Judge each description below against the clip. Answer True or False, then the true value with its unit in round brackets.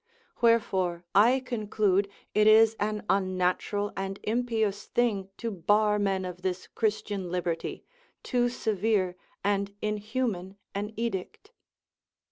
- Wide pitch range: False (2.7 semitones)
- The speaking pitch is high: True (205 Hz)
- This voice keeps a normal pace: False (110 wpm)